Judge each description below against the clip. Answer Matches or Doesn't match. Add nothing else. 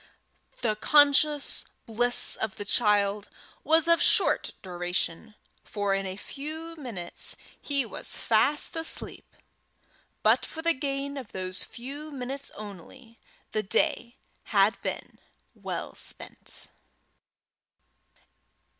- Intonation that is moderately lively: Doesn't match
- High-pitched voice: Matches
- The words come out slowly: Matches